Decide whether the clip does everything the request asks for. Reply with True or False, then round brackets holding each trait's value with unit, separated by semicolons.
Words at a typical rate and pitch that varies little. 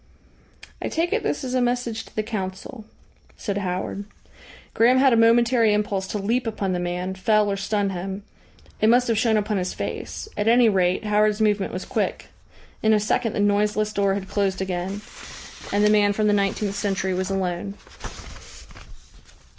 True (180 wpm; 2.3 semitones)